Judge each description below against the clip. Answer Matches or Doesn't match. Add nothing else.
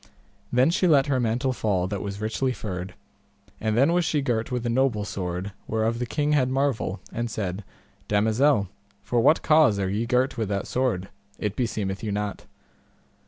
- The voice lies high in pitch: Doesn't match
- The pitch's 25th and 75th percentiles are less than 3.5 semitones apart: Doesn't match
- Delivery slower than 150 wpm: Doesn't match